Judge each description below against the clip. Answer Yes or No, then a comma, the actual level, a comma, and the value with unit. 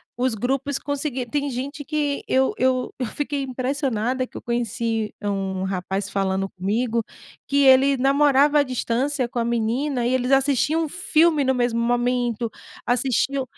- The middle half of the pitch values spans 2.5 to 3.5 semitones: Yes, average, 3.1 semitones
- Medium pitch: No, very high, 255 Hz